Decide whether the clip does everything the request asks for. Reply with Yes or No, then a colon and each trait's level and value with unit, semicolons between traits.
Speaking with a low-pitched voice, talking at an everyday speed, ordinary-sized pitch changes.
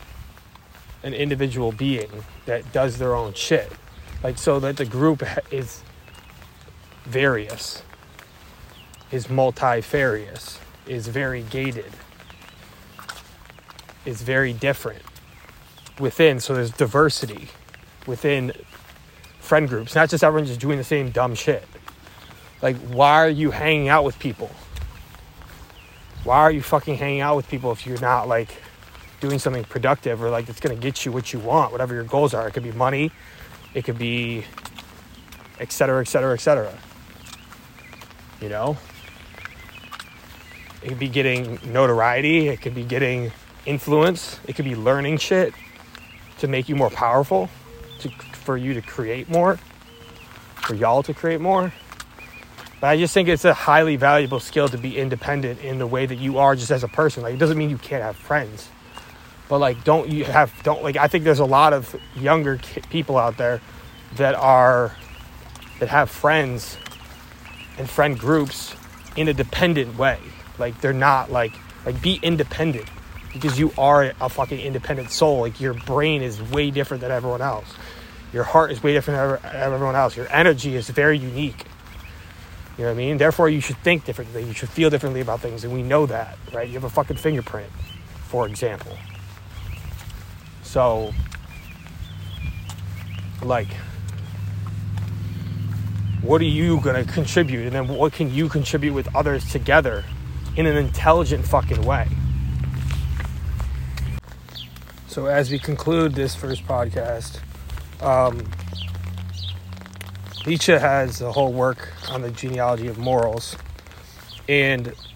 No: low, 125 Hz; average, 145 wpm; wide, 6.3 semitones